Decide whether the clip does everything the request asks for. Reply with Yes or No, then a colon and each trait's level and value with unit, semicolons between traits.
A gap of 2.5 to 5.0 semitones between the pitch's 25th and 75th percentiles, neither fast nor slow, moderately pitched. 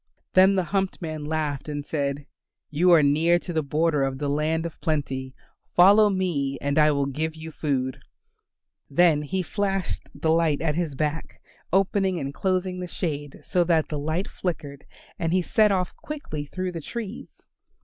Yes: average, 3.8 semitones; average, 175 wpm; medium, 160 Hz